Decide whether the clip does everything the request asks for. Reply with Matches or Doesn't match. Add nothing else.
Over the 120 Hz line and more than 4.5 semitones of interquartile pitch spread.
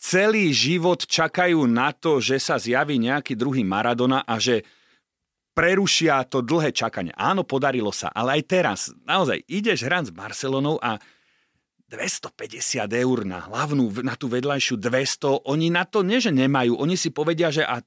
Matches